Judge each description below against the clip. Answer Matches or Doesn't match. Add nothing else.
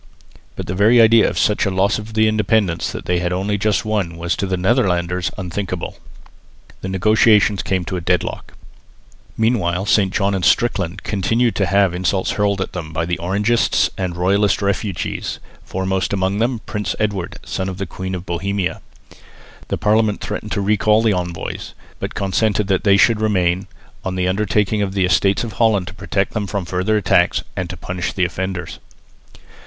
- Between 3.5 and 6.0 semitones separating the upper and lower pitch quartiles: Doesn't match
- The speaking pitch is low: Matches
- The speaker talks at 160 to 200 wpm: Matches